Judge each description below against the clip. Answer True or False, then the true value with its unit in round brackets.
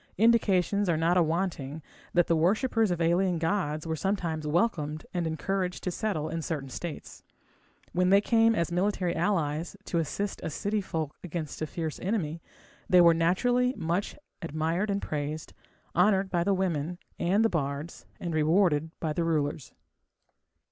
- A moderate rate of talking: True (155 wpm)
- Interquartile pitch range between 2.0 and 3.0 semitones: False (3.5 semitones)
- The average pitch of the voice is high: False (170 Hz)